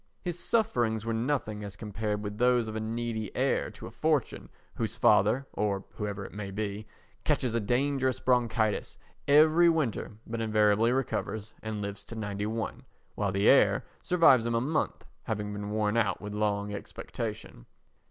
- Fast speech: No, average, 160 wpm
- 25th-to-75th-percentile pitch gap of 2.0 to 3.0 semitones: Yes, average, 2.7 semitones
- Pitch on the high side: No, low, 110 Hz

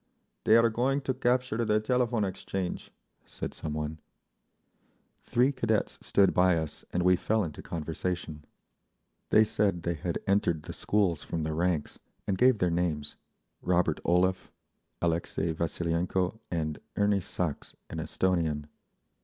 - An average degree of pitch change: Yes, average, 4.6 semitones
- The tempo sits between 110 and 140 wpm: Yes, slow, 135 wpm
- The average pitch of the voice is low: Yes, very low, 90 Hz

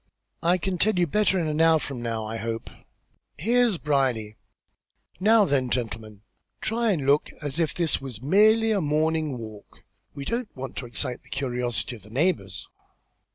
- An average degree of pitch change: No, wide, 7.2 semitones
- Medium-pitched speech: Yes, medium, 145 Hz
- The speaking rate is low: No, average, 170 wpm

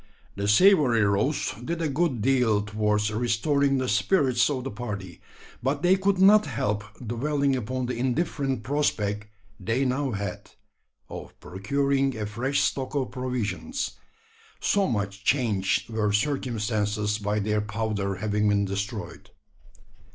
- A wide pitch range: No, average, 4.8 semitones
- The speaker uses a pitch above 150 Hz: No, low, 115 Hz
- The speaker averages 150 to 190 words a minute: No, slow, 135 wpm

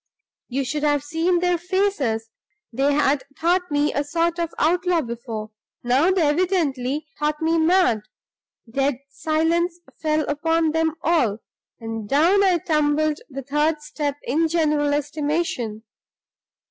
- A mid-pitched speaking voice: No, very high, 300 Hz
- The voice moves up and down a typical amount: Yes, average, 3.3 semitones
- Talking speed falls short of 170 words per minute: Yes, slow, 135 wpm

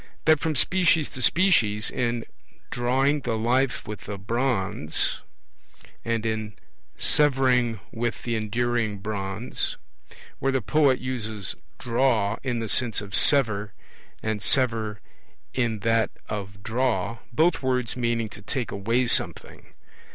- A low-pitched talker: Yes, low, 115 Hz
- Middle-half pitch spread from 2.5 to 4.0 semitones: Yes, average, 3.3 semitones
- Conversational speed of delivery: No, slow, 125 wpm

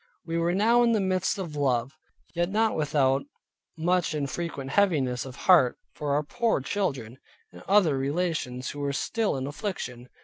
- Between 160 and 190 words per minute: Yes, average, 170 wpm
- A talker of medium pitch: Yes, medium, 155 Hz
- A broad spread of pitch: Yes, wide, 5.8 semitones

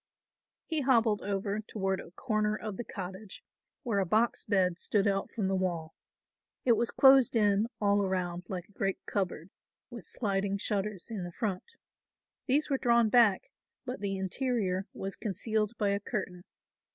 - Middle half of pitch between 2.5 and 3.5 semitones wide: Yes, average, 3.0 semitones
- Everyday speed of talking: Yes, average, 165 wpm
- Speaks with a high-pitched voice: Yes, high, 205 Hz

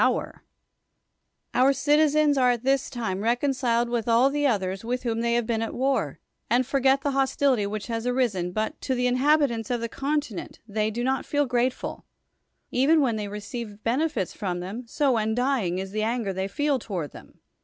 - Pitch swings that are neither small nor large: Yes, average, 3.9 semitones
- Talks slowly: No, average, 190 wpm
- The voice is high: Yes, high, 240 Hz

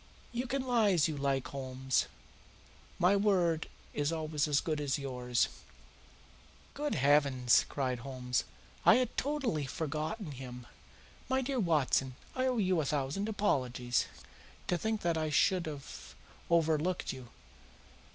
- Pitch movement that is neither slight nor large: No, wide, 6.9 semitones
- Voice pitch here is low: No, medium, 155 Hz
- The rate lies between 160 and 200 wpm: No, slow, 135 wpm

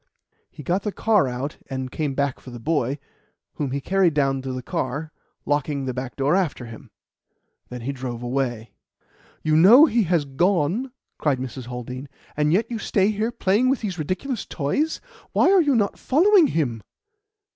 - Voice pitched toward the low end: No, medium, 150 Hz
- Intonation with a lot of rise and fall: Yes, wide, 7.5 semitones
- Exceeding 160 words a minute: Yes, average, 180 wpm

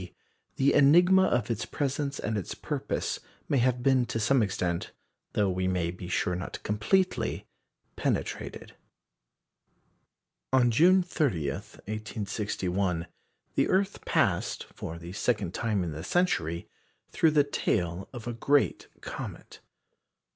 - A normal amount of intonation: No, wide, 7.5 semitones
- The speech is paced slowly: Yes, slow, 130 wpm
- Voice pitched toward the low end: Yes, low, 110 Hz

